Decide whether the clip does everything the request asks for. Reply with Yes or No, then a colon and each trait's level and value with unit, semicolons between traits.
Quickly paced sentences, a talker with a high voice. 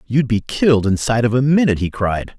No: fast, 225 wpm; low, 120 Hz